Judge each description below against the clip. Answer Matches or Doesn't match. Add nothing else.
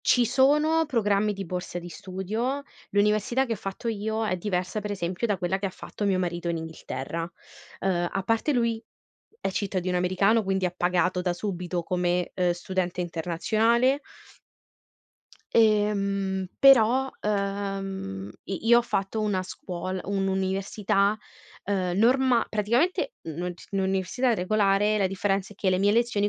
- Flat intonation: Doesn't match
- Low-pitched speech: Doesn't match